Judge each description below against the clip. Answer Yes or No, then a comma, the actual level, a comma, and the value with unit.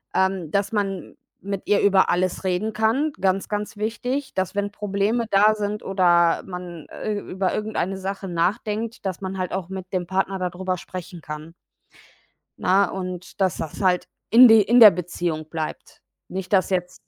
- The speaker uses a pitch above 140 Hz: Yes, high, 190 Hz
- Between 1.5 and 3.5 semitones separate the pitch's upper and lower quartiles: Yes, narrow, 2.5 semitones